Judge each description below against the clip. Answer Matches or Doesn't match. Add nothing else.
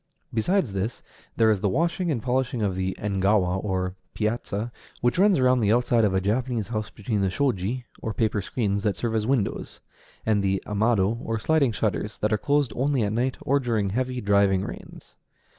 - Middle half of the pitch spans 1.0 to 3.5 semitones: Doesn't match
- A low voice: Matches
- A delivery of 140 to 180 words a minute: Doesn't match